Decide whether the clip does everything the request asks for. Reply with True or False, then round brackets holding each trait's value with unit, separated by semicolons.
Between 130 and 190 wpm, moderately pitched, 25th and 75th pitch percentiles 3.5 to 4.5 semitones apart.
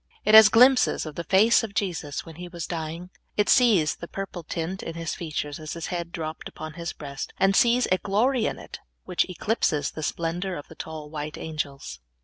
False (205 wpm; 170 Hz; 4.0 semitones)